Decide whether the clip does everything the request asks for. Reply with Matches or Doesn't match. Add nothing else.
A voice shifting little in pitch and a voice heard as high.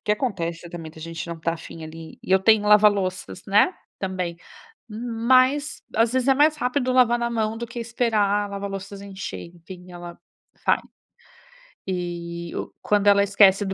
Doesn't match